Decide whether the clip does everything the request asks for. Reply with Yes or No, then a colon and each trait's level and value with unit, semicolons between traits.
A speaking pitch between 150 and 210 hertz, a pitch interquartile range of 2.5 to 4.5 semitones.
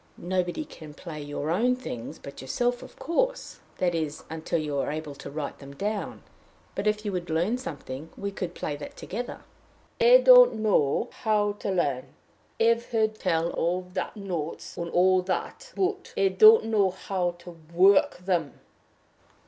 No: medium, 185 Hz; wide, 5.4 semitones